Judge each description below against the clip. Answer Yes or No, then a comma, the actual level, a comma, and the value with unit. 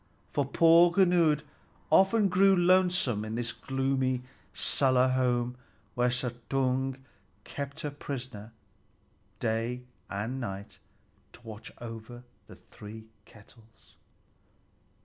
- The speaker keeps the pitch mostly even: No, average, 4.2 semitones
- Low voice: Yes, low, 130 Hz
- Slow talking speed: Yes, slow, 100 wpm